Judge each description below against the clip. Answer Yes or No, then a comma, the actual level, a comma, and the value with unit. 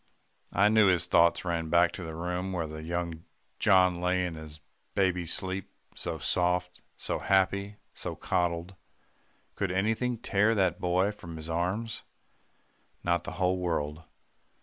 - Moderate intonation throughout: No, narrow, 2.1 semitones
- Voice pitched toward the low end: Yes, very low, 90 Hz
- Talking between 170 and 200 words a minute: No, average, 145 wpm